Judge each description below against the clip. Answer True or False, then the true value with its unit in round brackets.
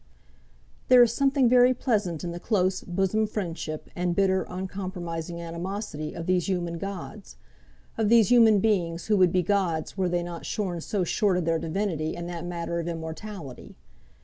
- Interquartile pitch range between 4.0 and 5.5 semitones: False (3.4 semitones)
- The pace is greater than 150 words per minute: True (170 wpm)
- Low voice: False (180 Hz)